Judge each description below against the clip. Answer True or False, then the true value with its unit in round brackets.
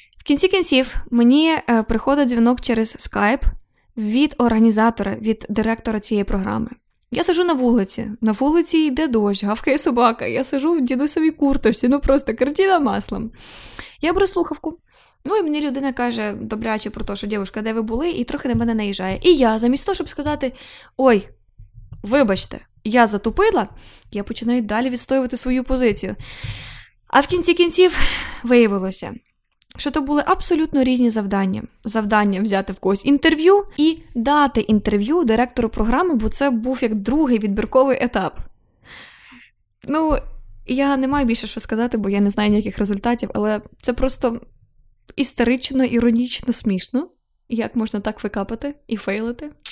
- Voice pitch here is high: True (240 Hz)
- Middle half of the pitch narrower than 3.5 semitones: False (4.7 semitones)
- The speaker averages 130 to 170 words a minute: True (150 wpm)